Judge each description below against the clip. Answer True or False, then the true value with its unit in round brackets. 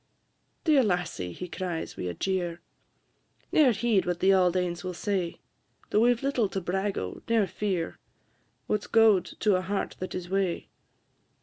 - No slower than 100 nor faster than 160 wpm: False (175 wpm)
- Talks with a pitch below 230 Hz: True (190 Hz)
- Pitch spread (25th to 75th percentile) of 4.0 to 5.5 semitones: False (3.0 semitones)